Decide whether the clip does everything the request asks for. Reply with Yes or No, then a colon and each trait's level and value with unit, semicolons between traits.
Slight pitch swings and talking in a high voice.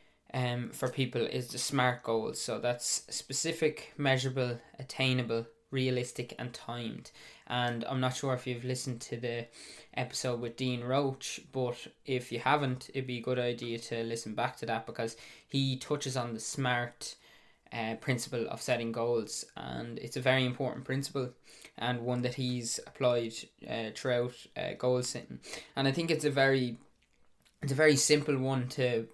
No: narrow, 2.0 semitones; low, 125 Hz